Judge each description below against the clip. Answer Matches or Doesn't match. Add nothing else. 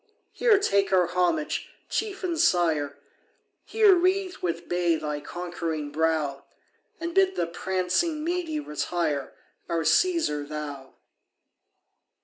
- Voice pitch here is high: Doesn't match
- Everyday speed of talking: Doesn't match